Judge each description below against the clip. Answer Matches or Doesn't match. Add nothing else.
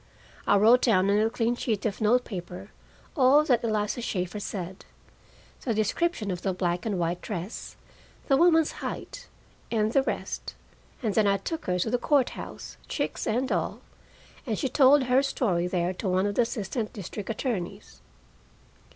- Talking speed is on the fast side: Doesn't match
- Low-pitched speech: Doesn't match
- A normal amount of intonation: Matches